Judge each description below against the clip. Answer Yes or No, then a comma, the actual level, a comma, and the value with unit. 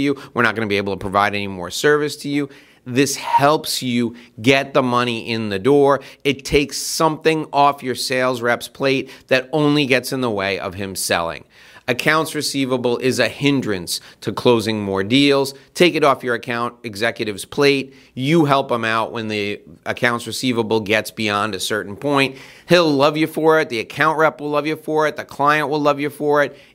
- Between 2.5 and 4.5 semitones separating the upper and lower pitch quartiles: Yes, average, 3.8 semitones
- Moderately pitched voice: No, low, 130 Hz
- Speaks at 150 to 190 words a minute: No, average, 200 wpm